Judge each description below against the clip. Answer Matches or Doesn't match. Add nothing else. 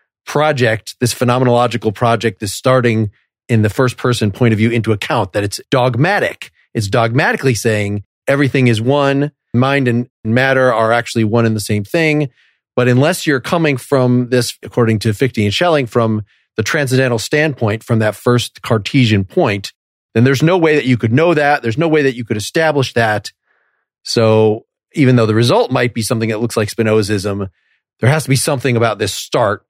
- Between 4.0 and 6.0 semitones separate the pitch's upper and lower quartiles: Doesn't match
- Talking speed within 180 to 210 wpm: Matches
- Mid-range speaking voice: Doesn't match